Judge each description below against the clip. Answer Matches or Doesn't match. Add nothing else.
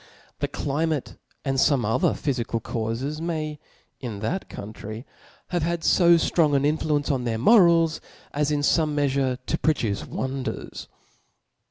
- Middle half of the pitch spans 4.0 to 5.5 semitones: Matches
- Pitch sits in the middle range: Matches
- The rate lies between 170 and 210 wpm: Doesn't match